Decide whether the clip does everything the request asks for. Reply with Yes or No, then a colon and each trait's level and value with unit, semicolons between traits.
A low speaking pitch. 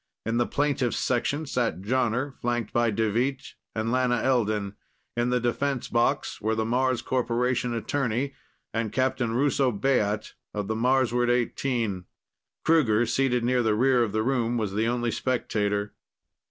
Yes: low, 120 Hz